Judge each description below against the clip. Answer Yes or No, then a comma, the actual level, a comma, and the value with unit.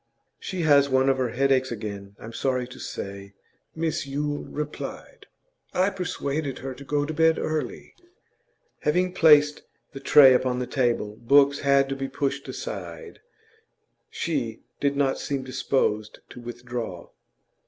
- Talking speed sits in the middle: Yes, average, 145 wpm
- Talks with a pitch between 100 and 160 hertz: Yes, low, 135 Hz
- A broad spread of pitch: No, average, 3.0 semitones